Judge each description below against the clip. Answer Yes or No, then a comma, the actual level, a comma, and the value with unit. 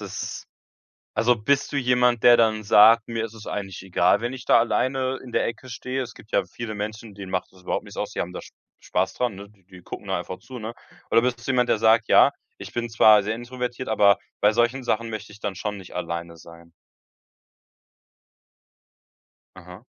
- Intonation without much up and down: No, average, 3.2 semitones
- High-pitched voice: No, low, 110 Hz